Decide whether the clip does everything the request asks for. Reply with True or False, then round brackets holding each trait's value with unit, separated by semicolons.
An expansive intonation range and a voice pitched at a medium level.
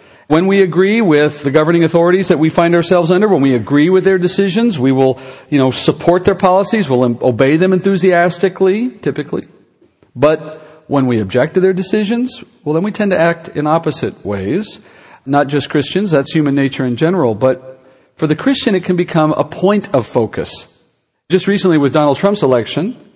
False (4.8 semitones; 165 Hz)